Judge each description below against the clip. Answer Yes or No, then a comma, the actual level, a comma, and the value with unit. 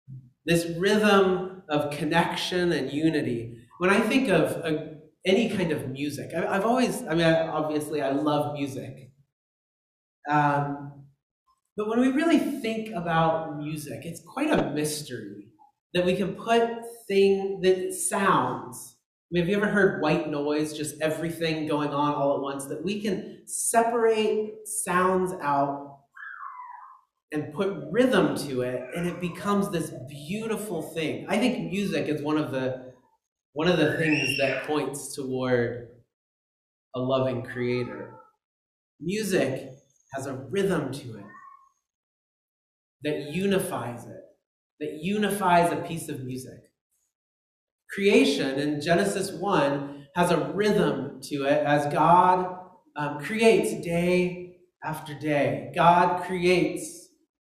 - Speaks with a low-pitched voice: No, medium, 165 Hz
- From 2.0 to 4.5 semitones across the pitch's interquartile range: No, wide, 5.6 semitones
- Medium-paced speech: No, slow, 130 wpm